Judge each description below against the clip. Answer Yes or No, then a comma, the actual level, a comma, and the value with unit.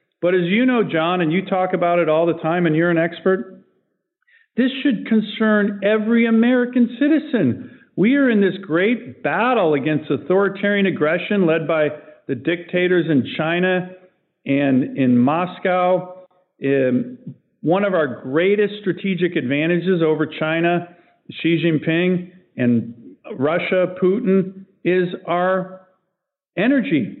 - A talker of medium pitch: Yes, medium, 180 Hz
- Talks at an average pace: No, slow, 130 wpm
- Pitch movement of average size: Yes, average, 3.3 semitones